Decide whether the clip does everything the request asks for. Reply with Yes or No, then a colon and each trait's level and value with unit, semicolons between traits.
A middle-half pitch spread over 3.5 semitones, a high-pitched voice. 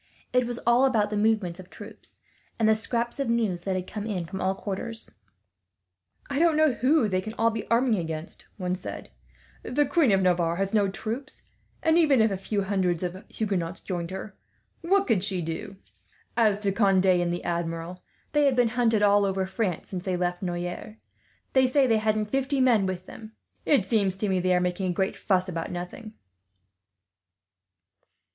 Yes: average, 4.1 semitones; high, 200 Hz